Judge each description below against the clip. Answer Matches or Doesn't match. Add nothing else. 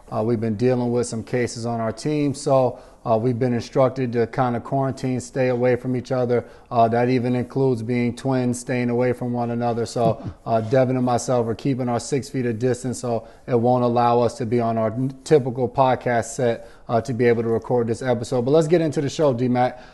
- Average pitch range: Doesn't match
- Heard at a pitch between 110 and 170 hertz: Matches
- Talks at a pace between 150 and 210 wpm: Doesn't match